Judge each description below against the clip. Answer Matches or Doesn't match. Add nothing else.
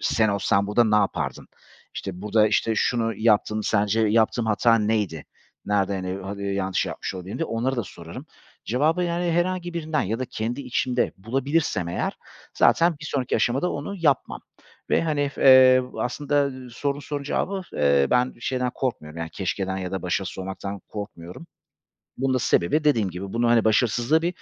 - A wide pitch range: Matches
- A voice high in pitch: Doesn't match